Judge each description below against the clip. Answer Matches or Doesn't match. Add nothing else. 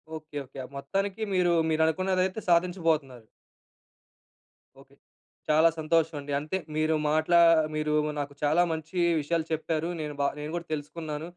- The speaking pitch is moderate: Matches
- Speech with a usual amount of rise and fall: Doesn't match